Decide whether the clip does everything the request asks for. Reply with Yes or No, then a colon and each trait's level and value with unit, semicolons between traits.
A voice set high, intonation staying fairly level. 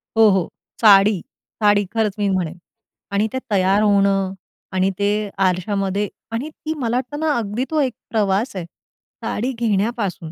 No: high, 205 Hz; average, 3.0 semitones